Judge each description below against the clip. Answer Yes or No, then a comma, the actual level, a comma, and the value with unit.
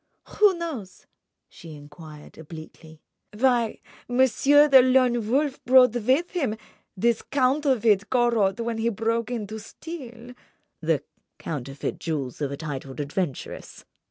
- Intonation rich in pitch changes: Yes, wide, 7.9 semitones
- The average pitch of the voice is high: Yes, high, 230 Hz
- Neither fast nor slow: No, slow, 125 wpm